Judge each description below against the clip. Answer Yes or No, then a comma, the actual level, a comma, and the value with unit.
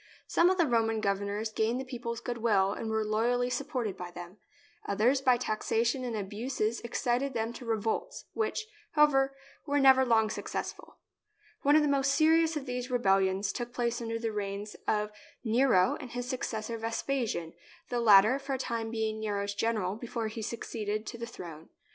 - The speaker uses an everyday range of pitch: Yes, average, 3.1 semitones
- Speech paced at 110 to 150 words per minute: No, average, 180 wpm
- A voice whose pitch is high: Yes, high, 230 Hz